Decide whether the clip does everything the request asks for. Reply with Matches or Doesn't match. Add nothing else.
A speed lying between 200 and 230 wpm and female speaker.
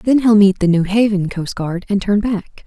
Matches